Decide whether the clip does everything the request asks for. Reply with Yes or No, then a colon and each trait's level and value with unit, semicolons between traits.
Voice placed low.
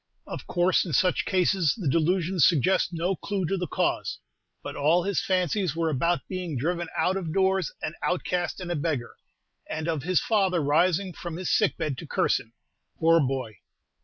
No: medium, 175 Hz